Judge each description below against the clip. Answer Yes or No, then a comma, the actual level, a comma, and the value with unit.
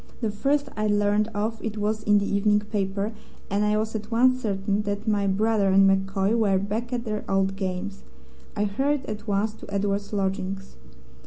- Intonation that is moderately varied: No, narrow, 1.7 semitones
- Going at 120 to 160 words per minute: No, average, 185 wpm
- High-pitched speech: Yes, high, 205 Hz